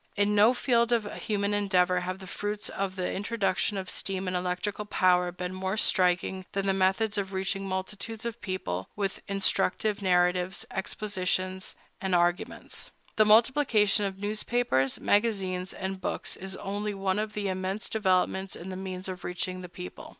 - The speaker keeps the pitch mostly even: Yes, narrow, 2.0 semitones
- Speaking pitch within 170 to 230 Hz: Yes, high, 190 Hz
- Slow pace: No, average, 165 wpm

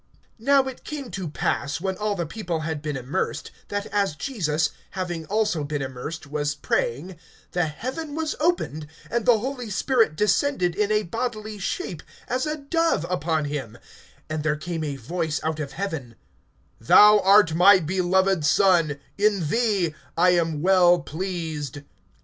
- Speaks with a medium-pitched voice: Yes, medium, 180 Hz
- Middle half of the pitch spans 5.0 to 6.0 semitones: Yes, wide, 5.6 semitones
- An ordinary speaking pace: Yes, average, 155 wpm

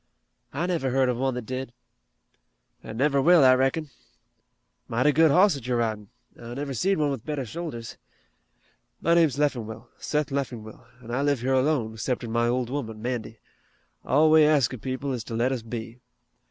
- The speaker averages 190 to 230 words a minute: No, average, 180 wpm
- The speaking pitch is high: No, low, 130 Hz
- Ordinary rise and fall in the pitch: Yes, average, 3.7 semitones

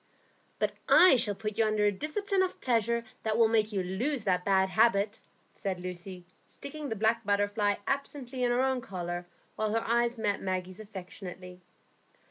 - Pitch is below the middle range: No, high, 215 Hz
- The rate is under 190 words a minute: Yes, average, 170 wpm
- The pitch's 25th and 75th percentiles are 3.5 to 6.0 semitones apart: Yes, average, 3.8 semitones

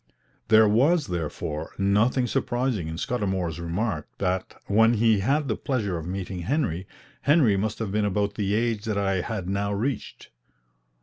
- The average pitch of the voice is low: Yes, low, 105 Hz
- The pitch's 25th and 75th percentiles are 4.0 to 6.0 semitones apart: No, average, 3.6 semitones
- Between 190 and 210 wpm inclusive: No, average, 160 wpm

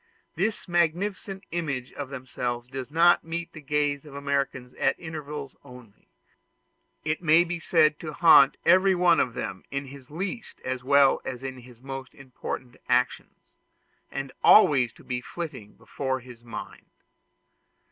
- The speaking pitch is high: No, medium, 140 Hz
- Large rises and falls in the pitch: No, average, 4.4 semitones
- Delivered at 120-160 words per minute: Yes, average, 150 wpm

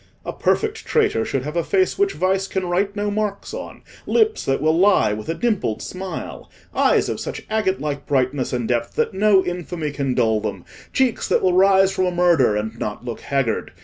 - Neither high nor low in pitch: Yes, medium, 175 Hz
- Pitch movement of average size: No, wide, 7.0 semitones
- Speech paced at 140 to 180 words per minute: No, average, 190 wpm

